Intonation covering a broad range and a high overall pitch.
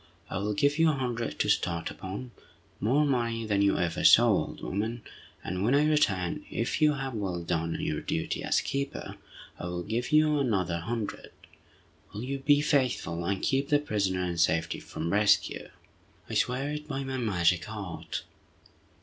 No: wide, 6.9 semitones; low, 110 Hz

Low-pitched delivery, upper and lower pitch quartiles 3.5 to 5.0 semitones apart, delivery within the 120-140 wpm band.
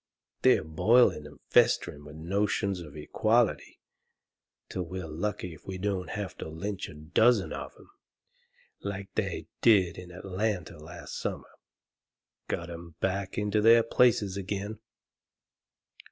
Yes: very low, 95 Hz; average, 3.8 semitones; slow, 135 wpm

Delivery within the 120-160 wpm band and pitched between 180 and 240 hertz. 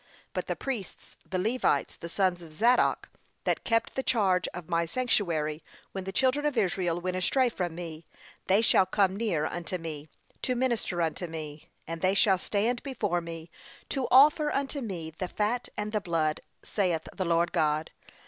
No: average, 175 wpm; medium, 185 Hz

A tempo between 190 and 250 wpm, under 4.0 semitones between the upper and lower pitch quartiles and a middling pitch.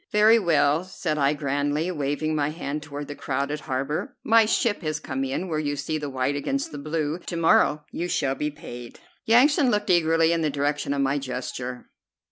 Yes: average, 195 wpm; average, 3.0 semitones; medium, 150 Hz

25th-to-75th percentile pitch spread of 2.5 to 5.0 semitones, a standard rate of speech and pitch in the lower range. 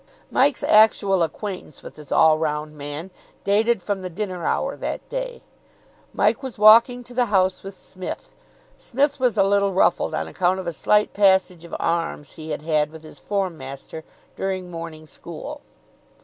No: average, 4.7 semitones; average, 170 wpm; high, 190 Hz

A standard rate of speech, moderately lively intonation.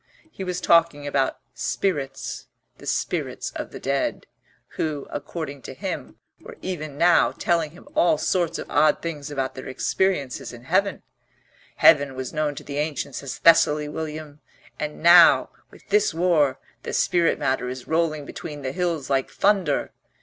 Yes: average, 155 wpm; average, 3.6 semitones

